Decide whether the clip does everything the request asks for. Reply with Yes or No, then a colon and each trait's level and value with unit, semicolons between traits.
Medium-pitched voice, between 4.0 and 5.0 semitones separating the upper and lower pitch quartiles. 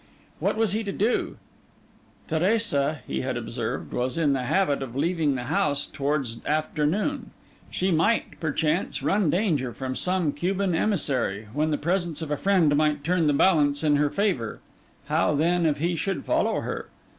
Yes: medium, 155 Hz; average, 4.3 semitones